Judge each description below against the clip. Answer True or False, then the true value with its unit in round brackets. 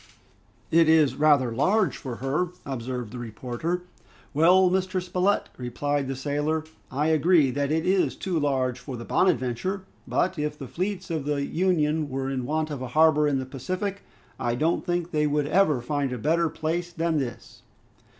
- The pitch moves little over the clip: False (4.4 semitones)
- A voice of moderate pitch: True (150 Hz)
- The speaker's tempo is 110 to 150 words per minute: False (175 wpm)